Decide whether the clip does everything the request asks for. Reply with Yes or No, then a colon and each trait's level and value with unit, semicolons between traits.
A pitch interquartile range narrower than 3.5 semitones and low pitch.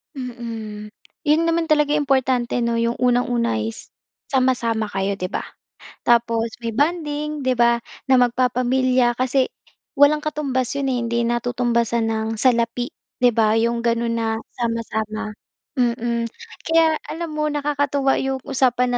No: average, 2.8 semitones; high, 245 Hz